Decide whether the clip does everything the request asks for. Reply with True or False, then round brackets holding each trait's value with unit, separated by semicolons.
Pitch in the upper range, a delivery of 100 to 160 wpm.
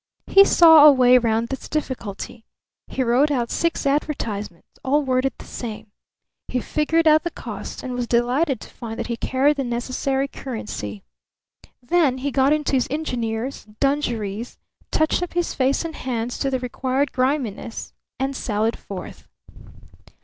True (260 Hz; 155 wpm)